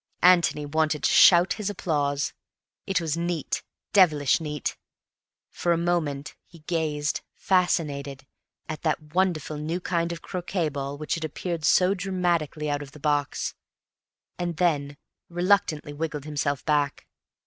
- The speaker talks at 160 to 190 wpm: No, slow, 135 wpm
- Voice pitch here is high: No, medium, 155 Hz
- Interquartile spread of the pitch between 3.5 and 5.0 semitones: No, average, 3.0 semitones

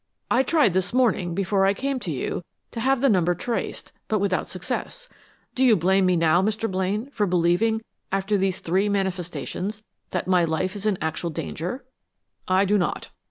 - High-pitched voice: Yes, high, 195 Hz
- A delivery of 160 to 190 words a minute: Yes, average, 180 wpm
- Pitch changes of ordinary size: Yes, average, 3.6 semitones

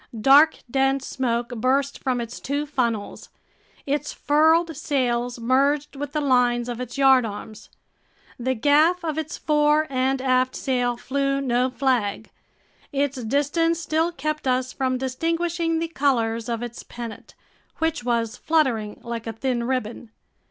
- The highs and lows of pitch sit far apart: No, average, 3.5 semitones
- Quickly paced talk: No, average, 140 wpm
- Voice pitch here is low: No, very high, 265 Hz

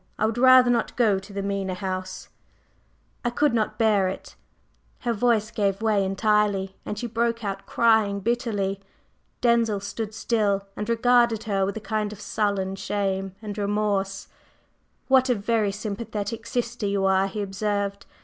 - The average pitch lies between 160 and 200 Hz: No, high, 210 Hz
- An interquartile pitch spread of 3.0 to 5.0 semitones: No, narrow, 2.6 semitones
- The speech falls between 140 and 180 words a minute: Yes, average, 160 wpm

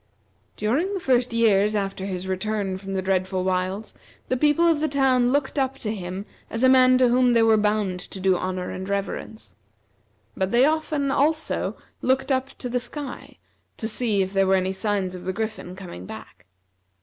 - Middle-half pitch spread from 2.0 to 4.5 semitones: No, wide, 5.4 semitones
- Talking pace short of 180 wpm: No, average, 190 wpm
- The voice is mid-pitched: No, high, 215 Hz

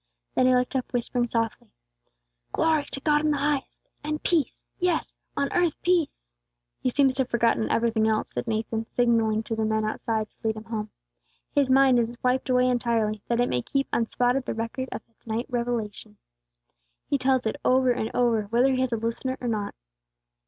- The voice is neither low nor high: No, high, 240 Hz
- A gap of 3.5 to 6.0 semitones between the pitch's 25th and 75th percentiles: No, average, 2.8 semitones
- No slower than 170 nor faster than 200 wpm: Yes, average, 195 wpm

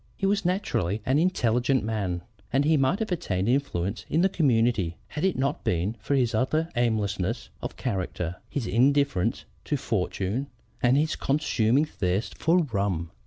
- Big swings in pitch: Yes, wide, 6.6 semitones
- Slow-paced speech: No, average, 160 wpm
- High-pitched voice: No, low, 120 Hz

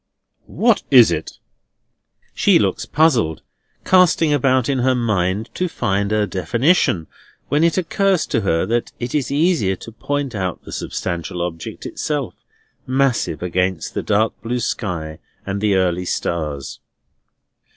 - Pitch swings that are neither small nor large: No, wide, 7.4 semitones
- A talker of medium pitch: No, low, 115 Hz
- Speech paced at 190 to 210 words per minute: No, average, 140 wpm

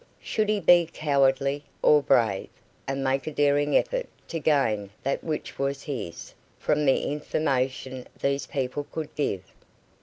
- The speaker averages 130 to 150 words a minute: Yes, average, 145 wpm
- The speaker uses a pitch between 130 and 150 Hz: Yes, medium, 140 Hz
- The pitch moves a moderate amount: No, narrow, 2.1 semitones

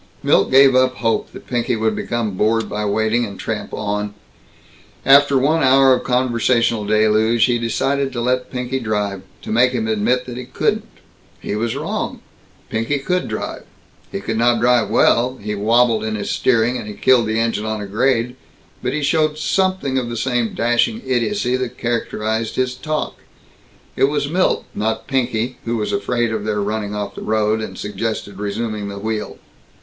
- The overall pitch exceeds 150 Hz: No, low, 115 Hz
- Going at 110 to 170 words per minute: No, average, 180 wpm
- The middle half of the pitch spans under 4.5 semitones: Yes, average, 2.9 semitones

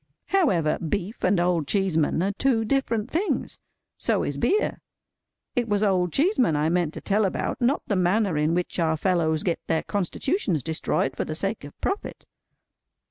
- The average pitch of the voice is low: No, medium, 185 Hz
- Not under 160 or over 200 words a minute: Yes, average, 170 wpm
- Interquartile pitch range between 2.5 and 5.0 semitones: No, wide, 5.5 semitones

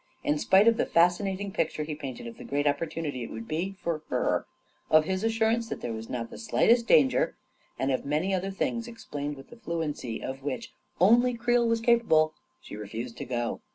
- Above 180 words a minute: Yes, average, 200 wpm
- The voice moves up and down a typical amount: No, wide, 8.7 semitones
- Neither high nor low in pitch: Yes, medium, 165 Hz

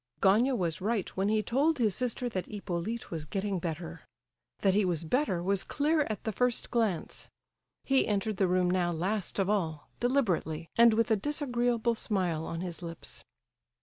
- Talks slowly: No, average, 175 wpm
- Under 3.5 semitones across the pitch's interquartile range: No, average, 4.9 semitones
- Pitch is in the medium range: No, high, 200 Hz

